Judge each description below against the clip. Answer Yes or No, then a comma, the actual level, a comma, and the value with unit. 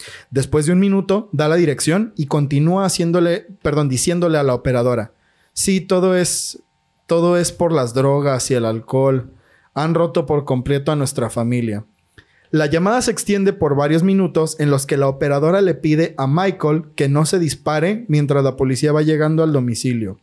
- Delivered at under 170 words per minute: No, average, 180 wpm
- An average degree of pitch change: Yes, average, 4.3 semitones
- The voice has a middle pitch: Yes, medium, 150 Hz